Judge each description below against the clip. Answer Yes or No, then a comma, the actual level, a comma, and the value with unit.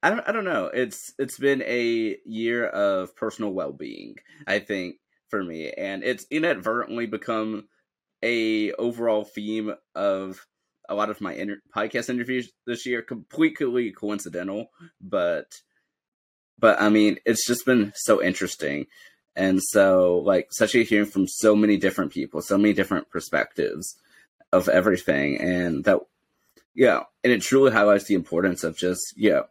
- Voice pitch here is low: Yes, low, 105 Hz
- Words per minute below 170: Yes, average, 160 wpm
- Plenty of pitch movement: No, average, 3.3 semitones